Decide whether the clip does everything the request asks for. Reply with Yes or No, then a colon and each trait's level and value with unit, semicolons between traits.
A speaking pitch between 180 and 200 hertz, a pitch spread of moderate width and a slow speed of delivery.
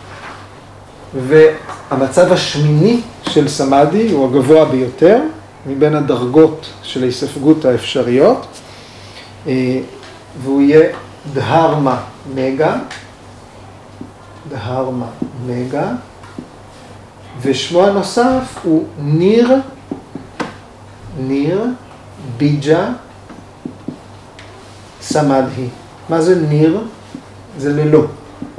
No: low, 135 Hz; average, 4.5 semitones; slow, 65 wpm